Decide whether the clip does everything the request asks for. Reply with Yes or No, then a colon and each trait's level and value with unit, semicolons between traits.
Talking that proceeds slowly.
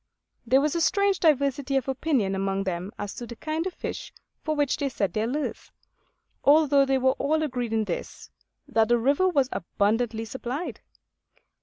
No: average, 175 wpm